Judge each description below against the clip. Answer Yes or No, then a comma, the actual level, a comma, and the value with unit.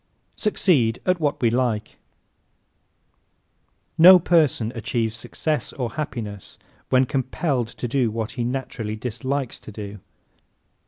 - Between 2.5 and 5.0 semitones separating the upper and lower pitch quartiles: Yes, average, 4.1 semitones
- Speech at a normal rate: No, slow, 120 wpm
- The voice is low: Yes, low, 125 Hz